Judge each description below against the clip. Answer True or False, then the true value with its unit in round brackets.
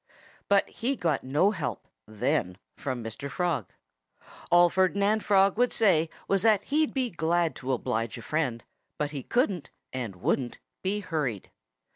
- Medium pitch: True (165 Hz)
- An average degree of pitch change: False (7.6 semitones)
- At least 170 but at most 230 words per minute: False (150 wpm)